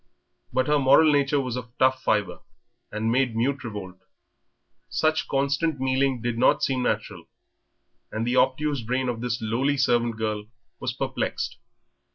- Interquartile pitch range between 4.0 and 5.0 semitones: No, average, 3.3 semitones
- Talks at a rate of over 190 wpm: No, average, 150 wpm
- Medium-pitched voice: No, low, 125 Hz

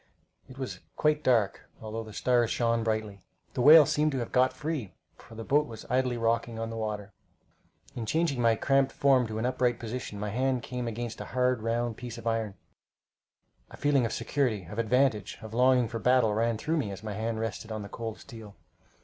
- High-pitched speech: No, low, 115 Hz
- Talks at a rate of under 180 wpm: No, fast, 205 wpm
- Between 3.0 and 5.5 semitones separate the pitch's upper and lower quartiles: No, narrow, 2.6 semitones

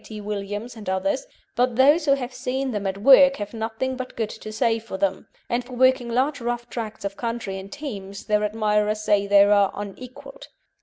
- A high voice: Yes, high, 225 Hz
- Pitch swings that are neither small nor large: Yes, average, 3.6 semitones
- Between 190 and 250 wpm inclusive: Yes, average, 200 wpm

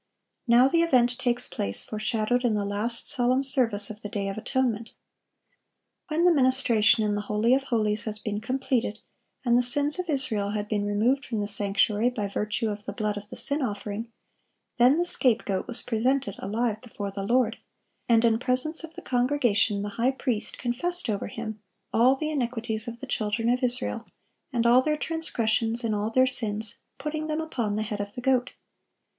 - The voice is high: Yes, high, 235 Hz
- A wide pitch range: No, average, 3.5 semitones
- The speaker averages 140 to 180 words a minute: No, average, 190 wpm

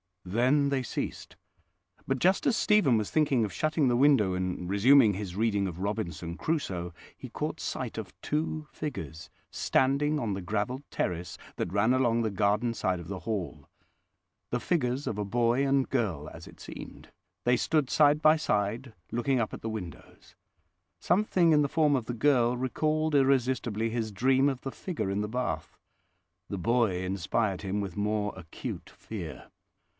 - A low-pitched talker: Yes, low, 115 Hz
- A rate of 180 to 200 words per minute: No, average, 170 wpm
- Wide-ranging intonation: Yes, wide, 5.8 semitones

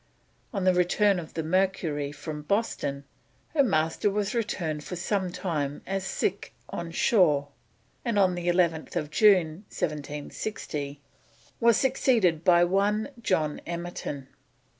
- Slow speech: Yes, slow, 120 wpm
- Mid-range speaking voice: Yes, medium, 175 Hz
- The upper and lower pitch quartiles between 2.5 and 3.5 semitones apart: No, average, 4.4 semitones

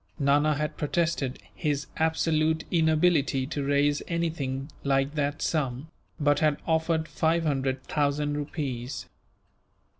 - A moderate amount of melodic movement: No, narrow, 2.3 semitones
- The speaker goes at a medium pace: No, slow, 115 wpm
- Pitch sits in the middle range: Yes, medium, 150 Hz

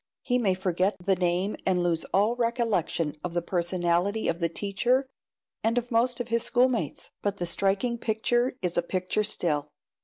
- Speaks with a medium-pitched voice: No, high, 195 Hz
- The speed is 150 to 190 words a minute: Yes, average, 175 wpm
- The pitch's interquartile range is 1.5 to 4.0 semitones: No, average, 5.0 semitones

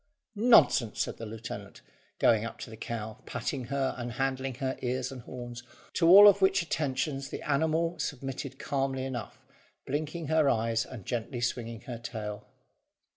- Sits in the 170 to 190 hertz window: No, low, 130 Hz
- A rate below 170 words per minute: Yes, average, 160 wpm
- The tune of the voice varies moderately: Yes, average, 3.5 semitones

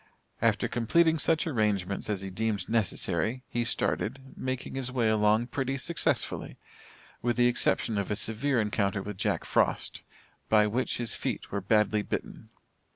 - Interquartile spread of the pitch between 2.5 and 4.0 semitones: Yes, average, 3.6 semitones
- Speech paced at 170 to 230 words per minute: No, average, 155 wpm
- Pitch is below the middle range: Yes, low, 115 Hz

